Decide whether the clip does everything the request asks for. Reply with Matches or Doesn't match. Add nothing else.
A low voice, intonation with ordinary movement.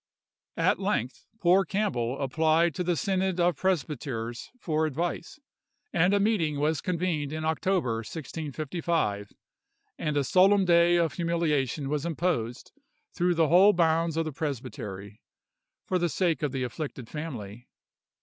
Doesn't match